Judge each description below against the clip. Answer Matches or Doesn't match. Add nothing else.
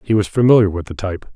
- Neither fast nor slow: Doesn't match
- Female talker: Doesn't match